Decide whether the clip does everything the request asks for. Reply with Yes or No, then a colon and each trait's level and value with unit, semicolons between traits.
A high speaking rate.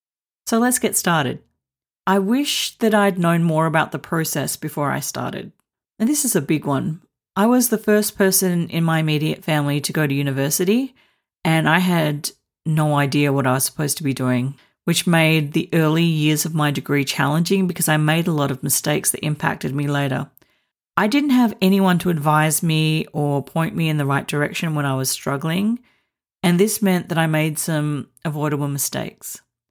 No: average, 190 wpm